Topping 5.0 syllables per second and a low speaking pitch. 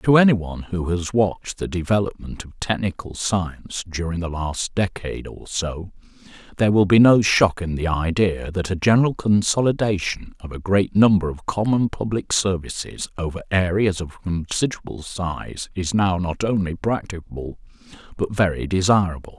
No: 4.9 syllables/s; very low, 95 Hz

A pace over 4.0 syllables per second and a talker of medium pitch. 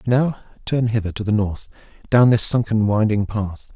No: 5.0 syllables/s; low, 110 Hz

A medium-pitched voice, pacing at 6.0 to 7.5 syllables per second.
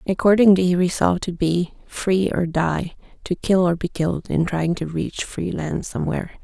No: medium, 175 Hz; 5.0 syllables/s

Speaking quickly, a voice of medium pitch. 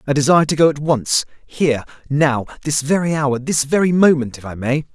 No: average, 160 wpm; medium, 145 Hz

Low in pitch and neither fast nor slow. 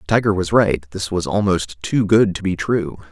No: very low, 95 Hz; fast, 210 wpm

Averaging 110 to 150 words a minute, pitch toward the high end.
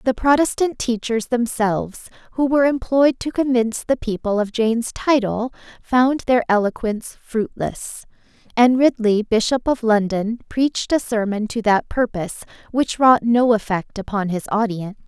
Yes: average, 145 wpm; high, 230 Hz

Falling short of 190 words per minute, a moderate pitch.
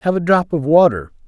No: fast, 235 wpm; medium, 155 Hz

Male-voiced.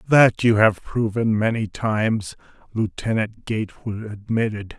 Yes: male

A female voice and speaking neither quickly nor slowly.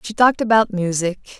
Yes: female; average, 170 wpm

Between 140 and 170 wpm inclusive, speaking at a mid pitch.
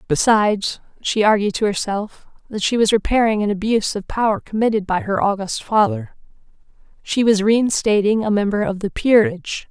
No: average, 160 wpm; high, 215 Hz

